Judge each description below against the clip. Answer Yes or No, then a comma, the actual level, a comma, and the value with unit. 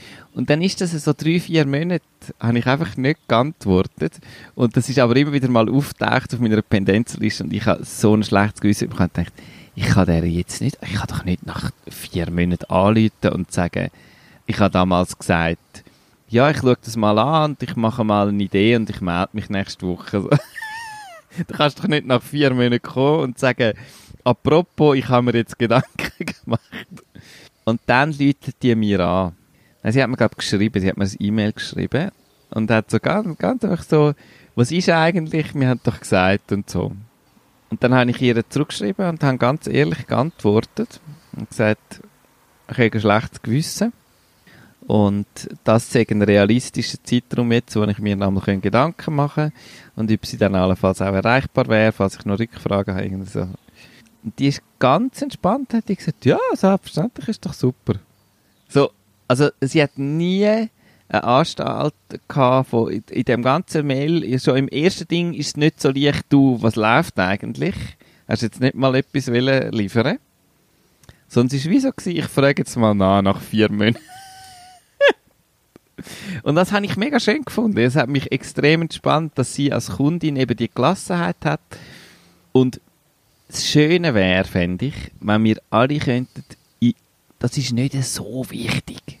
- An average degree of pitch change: No, wide, 5.9 semitones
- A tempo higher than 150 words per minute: Yes, average, 180 wpm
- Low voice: Yes, low, 125 Hz